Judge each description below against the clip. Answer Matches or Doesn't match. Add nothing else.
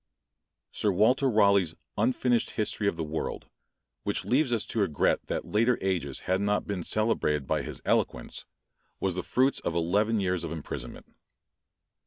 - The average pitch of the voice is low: Matches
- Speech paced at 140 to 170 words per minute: Matches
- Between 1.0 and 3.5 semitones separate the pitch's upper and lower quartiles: Doesn't match